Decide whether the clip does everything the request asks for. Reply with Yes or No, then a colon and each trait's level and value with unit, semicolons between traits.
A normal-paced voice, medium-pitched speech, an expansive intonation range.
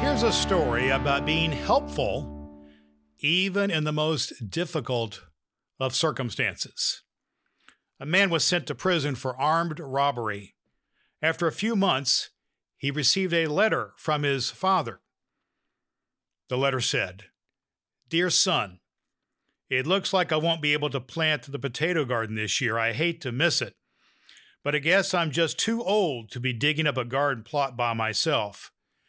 Yes: average, 150 wpm; medium, 145 Hz; wide, 5.7 semitones